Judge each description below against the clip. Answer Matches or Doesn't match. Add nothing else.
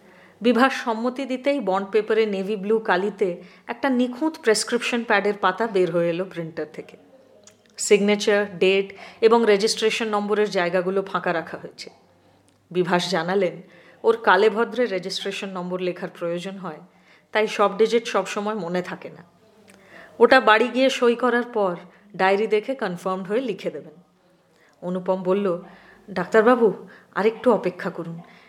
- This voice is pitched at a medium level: Doesn't match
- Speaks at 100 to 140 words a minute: Matches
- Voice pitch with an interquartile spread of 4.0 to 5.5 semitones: Doesn't match